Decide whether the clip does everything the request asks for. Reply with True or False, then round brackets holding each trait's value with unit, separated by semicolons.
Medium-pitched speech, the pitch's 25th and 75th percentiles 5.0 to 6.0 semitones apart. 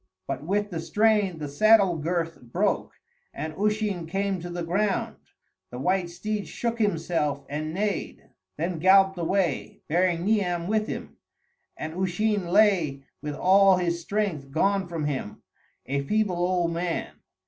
False (180 Hz; 3.7 semitones)